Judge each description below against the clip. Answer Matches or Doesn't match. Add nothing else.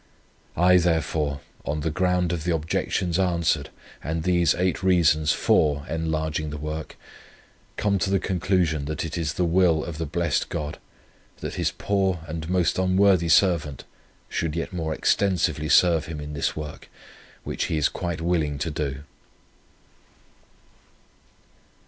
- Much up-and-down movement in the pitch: Doesn't match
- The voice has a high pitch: Doesn't match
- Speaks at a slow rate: Doesn't match